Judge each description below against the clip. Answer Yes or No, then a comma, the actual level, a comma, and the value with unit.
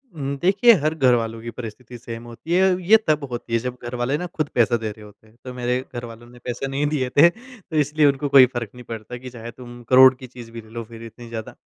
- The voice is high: No, low, 125 Hz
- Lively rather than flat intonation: No, average, 3.3 semitones